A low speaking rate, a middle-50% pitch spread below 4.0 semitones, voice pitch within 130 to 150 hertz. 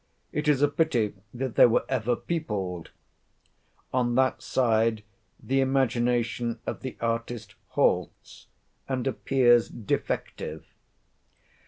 No: slow, 110 wpm; narrow, 2.6 semitones; low, 120 Hz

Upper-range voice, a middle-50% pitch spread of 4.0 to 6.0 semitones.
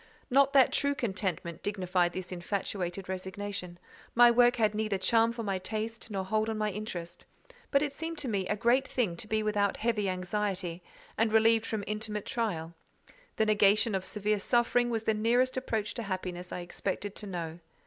No: high, 210 Hz; average, 3.4 semitones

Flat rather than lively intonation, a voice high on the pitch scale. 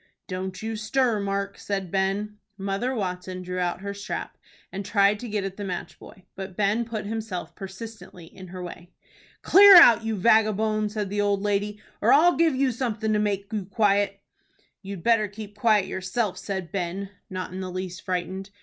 Yes: narrow, 2.3 semitones; high, 200 Hz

